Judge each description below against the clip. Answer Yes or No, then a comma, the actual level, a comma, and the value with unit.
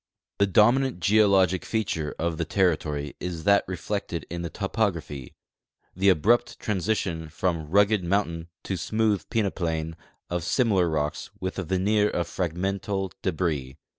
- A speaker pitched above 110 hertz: No, very low, 90 Hz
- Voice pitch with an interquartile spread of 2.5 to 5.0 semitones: Yes, average, 3.6 semitones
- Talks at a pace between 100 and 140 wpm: Yes, slow, 135 wpm